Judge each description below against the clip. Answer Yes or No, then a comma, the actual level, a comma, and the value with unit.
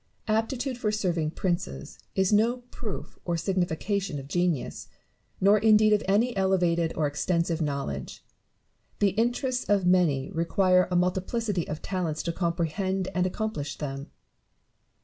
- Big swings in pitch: No, average, 4.1 semitones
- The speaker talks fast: No, slow, 135 wpm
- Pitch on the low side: No, medium, 185 Hz